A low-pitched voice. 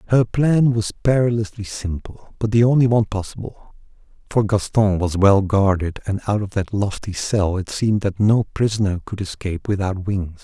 Yes: low, 105 Hz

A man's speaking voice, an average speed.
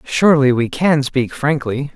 Yes: male; average, 155 wpm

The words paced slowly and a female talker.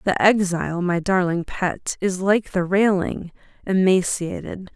Yes: slow, 125 wpm; female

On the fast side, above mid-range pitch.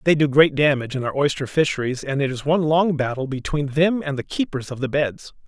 No: fast, 240 wpm; medium, 145 Hz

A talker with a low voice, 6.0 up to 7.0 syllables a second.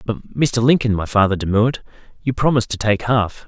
Yes: low, 115 Hz; 6.1 syllables/s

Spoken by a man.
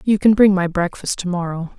No: female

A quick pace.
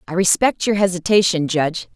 No: average, 155 wpm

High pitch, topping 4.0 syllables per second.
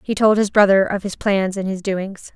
Yes: high, 195 Hz; 4.9 syllables/s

